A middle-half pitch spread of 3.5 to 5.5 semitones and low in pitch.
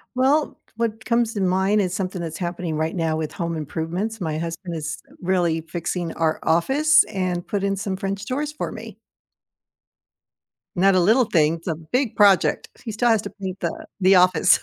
No: average, 4.2 semitones; medium, 185 Hz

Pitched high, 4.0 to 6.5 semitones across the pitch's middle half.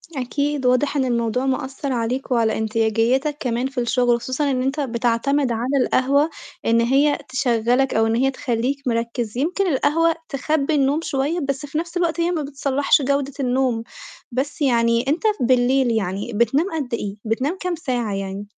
No: very high, 260 Hz; average, 3.3 semitones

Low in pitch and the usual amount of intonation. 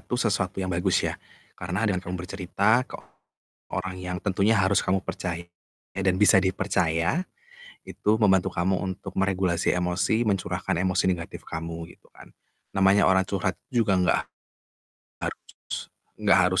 No: very low, 95 Hz; narrow, 1.5 semitones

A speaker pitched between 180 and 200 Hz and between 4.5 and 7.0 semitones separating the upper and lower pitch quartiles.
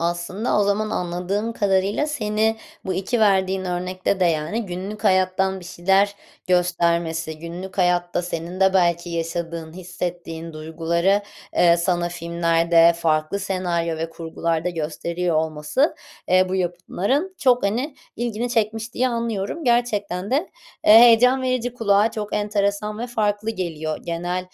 No: medium, 185 Hz; average, 3.8 semitones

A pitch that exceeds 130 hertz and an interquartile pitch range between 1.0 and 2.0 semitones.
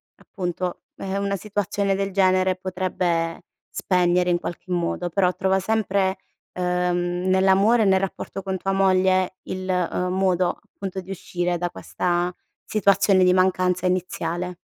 Yes: medium, 185 Hz; narrow, 1.3 semitones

